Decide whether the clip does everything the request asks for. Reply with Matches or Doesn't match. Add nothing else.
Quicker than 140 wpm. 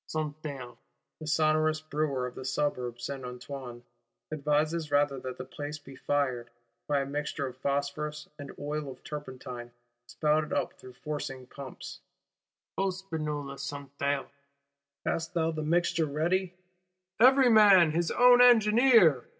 Doesn't match